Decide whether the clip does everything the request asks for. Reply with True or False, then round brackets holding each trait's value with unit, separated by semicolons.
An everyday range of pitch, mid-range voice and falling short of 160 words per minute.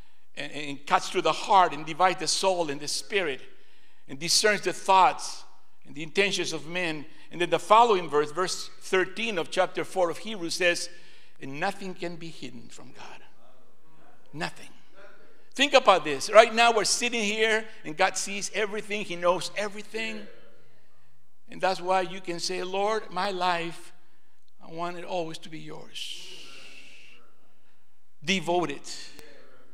True (3.8 semitones; 180 Hz; 150 wpm)